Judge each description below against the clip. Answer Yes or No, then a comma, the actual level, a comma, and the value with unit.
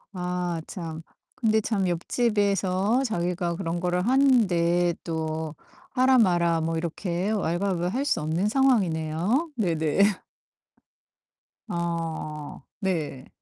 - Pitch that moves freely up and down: No, average, 4.0 semitones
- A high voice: No, medium, 175 Hz